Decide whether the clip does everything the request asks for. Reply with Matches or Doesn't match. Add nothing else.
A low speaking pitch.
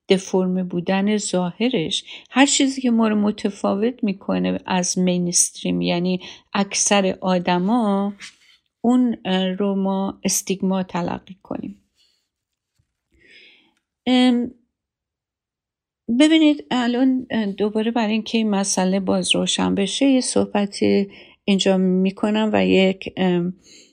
Doesn't match